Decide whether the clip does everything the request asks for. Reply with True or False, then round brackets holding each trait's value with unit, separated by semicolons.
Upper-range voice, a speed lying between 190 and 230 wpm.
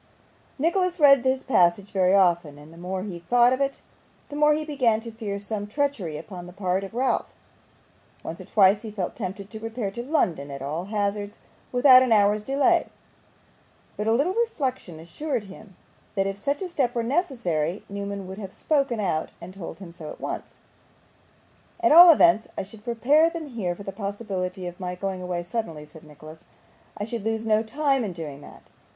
True (210 Hz; 195 wpm)